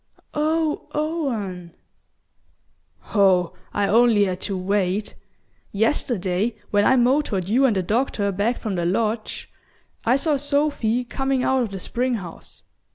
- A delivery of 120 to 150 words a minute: Yes, slow, 135 wpm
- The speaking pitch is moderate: No, high, 220 Hz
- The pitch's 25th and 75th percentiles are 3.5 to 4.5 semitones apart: No, average, 5.2 semitones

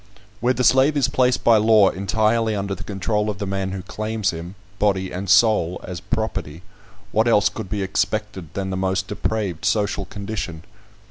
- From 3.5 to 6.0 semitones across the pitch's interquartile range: No, narrow, 2.5 semitones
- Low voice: Yes, low, 100 Hz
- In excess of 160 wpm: Yes, average, 180 wpm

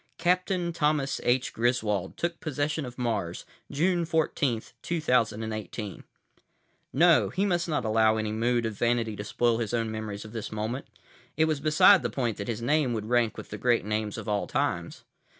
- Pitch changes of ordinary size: No, wide, 5.7 semitones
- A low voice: Yes, low, 120 Hz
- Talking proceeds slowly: No, average, 175 wpm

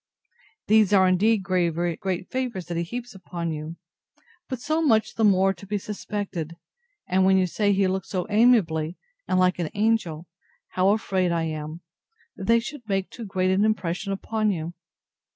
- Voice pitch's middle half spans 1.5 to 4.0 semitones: Yes, average, 3.7 semitones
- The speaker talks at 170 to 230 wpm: Yes, average, 175 wpm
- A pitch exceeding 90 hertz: Yes, high, 190 Hz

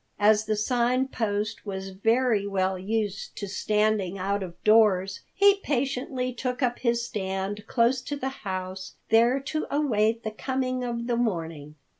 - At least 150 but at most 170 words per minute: Yes, average, 155 wpm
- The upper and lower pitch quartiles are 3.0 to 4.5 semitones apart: Yes, average, 4.2 semitones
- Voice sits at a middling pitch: No, high, 220 Hz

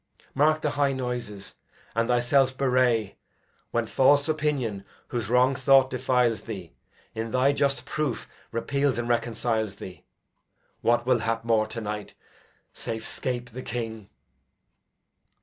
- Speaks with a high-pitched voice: No, low, 120 Hz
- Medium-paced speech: No, slow, 130 wpm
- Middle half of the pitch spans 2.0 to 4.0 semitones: Yes, average, 2.8 semitones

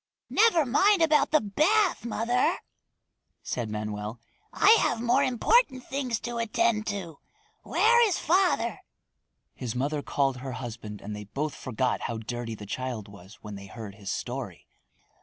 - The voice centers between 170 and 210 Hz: No, medium, 150 Hz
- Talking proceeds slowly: No, average, 150 wpm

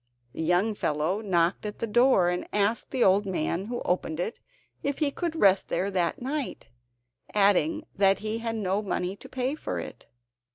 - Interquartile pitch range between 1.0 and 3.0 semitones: No, average, 4.7 semitones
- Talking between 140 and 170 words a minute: No, average, 180 wpm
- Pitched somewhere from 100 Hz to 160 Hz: No, high, 205 Hz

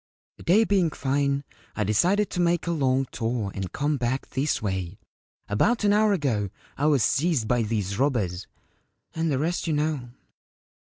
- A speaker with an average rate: Yes, average, 170 wpm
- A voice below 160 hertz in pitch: Yes, medium, 140 Hz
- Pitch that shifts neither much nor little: No, wide, 6.8 semitones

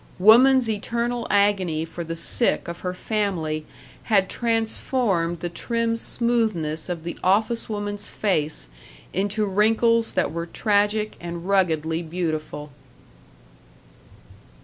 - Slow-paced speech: Yes, slow, 110 wpm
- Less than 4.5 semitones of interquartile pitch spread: No, average, 5.0 semitones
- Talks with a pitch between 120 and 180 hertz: No, high, 200 Hz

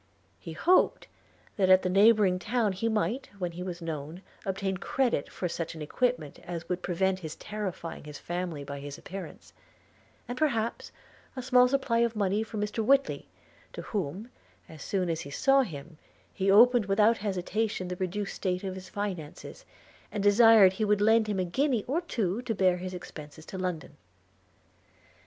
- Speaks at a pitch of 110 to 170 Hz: No, high, 195 Hz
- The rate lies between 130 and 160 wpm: No, average, 175 wpm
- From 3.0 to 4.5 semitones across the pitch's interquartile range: Yes, average, 4.0 semitones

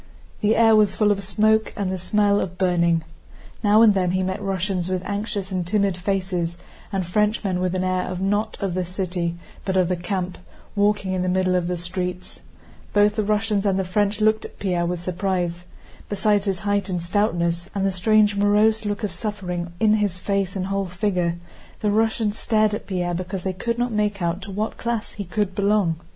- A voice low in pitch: No, high, 195 Hz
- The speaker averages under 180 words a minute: No, average, 200 wpm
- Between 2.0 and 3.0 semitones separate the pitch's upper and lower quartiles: Yes, narrow, 2.5 semitones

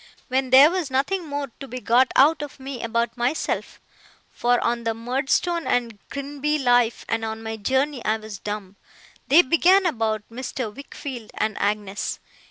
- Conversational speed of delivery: Yes, average, 165 wpm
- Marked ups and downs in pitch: No, average, 4.0 semitones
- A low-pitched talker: No, very high, 250 Hz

